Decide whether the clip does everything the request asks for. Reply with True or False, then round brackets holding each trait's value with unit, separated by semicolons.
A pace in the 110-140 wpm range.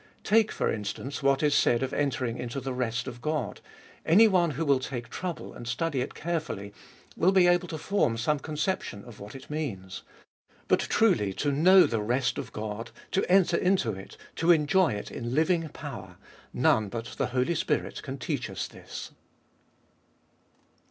False (175 wpm)